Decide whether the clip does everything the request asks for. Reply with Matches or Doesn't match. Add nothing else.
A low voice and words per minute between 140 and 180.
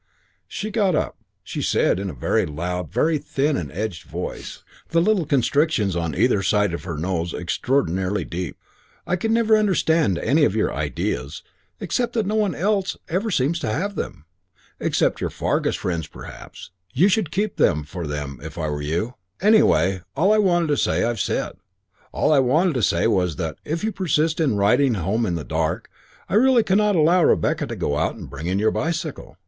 Doesn't match